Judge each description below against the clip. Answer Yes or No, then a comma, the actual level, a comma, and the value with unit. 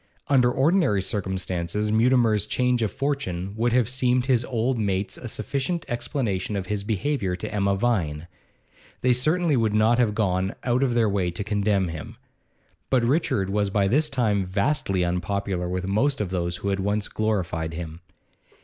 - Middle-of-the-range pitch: No, low, 105 Hz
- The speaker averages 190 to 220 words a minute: No, average, 170 wpm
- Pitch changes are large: No, average, 4.6 semitones